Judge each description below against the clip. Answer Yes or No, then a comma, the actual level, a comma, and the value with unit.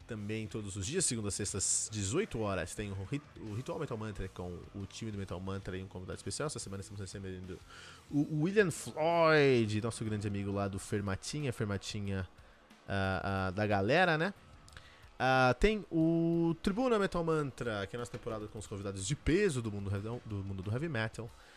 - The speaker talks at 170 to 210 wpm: Yes, average, 180 wpm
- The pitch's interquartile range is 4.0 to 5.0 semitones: Yes, average, 4.6 semitones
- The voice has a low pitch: Yes, low, 105 Hz